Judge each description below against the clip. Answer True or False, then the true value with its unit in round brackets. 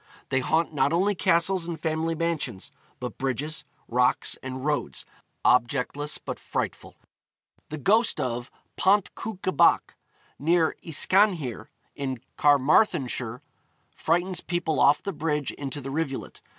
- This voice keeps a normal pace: False (125 wpm)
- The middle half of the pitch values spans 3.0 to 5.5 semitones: True (4.4 semitones)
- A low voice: False (150 Hz)